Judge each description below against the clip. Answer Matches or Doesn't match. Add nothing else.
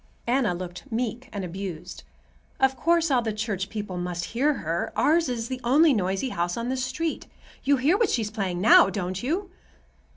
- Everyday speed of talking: Matches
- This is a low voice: Doesn't match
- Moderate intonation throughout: Doesn't match